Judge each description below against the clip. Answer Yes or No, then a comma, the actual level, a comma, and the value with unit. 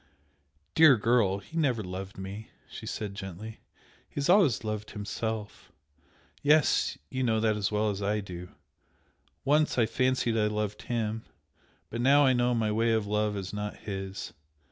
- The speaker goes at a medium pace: Yes, average, 165 wpm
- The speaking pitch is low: Yes, low, 110 Hz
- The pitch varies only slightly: No, average, 3.0 semitones